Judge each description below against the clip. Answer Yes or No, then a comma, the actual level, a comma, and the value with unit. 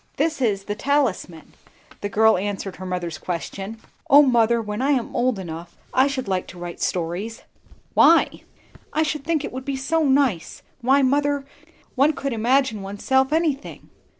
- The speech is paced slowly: No, average, 165 wpm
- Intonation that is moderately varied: No, wide, 6.1 semitones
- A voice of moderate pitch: No, high, 240 Hz